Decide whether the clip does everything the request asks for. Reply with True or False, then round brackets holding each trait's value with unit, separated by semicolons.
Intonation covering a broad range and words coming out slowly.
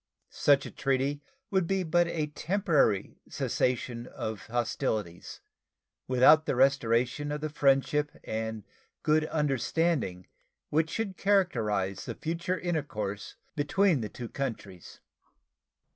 True (6.0 semitones; 115 wpm)